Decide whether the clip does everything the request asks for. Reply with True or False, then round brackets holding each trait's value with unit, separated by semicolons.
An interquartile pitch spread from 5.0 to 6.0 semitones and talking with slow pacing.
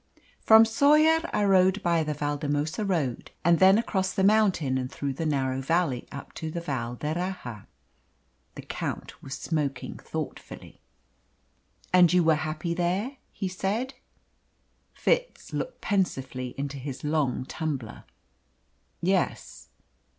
True (5.6 semitones; 130 wpm)